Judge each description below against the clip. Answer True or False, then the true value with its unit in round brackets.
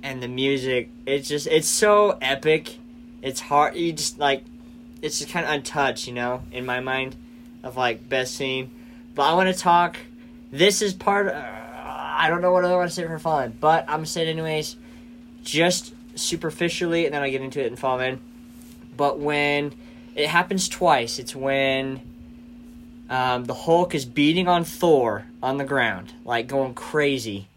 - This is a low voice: False (155 Hz)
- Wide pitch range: True (7.4 semitones)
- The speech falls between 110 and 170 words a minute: False (185 wpm)